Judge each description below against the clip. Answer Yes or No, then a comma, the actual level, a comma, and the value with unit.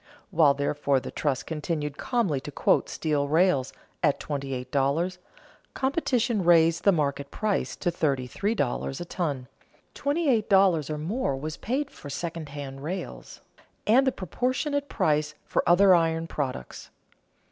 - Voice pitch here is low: No, medium, 160 Hz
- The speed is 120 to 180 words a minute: Yes, average, 150 wpm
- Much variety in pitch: Yes, wide, 5.7 semitones